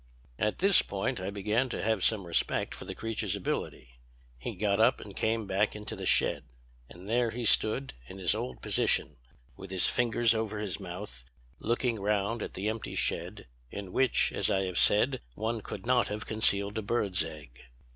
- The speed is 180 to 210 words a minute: Yes, average, 185 wpm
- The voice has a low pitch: Yes, low, 105 Hz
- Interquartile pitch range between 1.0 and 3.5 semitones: Yes, average, 2.9 semitones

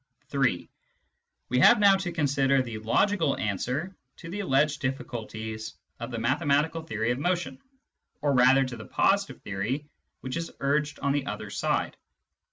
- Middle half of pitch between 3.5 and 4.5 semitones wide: No, average, 5.0 semitones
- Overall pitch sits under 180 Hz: Yes, low, 135 Hz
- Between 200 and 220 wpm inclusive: No, average, 155 wpm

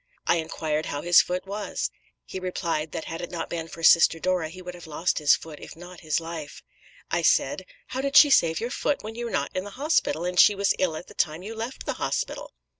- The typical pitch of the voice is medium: Yes, medium, 175 Hz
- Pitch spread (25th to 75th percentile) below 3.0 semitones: No, average, 3.6 semitones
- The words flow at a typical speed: No, fast, 245 wpm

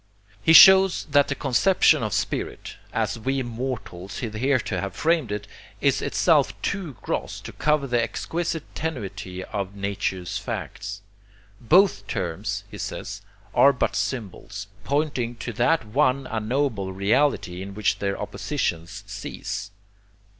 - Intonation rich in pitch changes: Yes, wide, 6.3 semitones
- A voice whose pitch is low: Yes, low, 120 Hz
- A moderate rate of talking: No, slow, 130 wpm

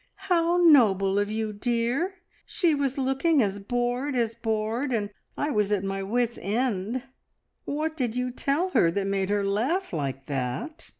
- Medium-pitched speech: No, high, 235 Hz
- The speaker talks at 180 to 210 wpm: No, average, 165 wpm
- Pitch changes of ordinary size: No, wide, 5.8 semitones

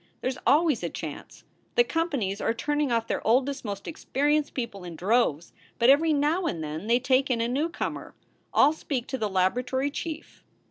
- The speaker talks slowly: No, average, 190 wpm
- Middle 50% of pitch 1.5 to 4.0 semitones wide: No, average, 4.9 semitones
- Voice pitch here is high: Yes, very high, 255 Hz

